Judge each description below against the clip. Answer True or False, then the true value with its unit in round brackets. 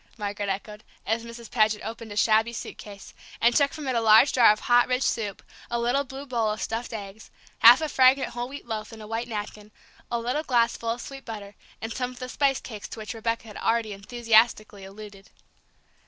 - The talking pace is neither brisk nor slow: False (215 wpm)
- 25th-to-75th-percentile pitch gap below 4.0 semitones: True (2.4 semitones)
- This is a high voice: True (230 Hz)